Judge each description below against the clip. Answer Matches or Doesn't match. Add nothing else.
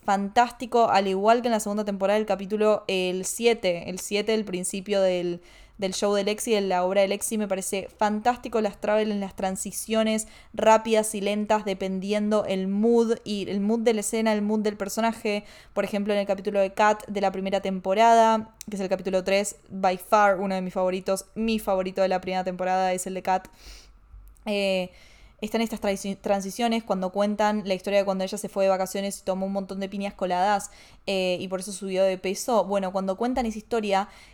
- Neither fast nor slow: Doesn't match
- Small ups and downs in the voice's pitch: Matches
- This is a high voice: Matches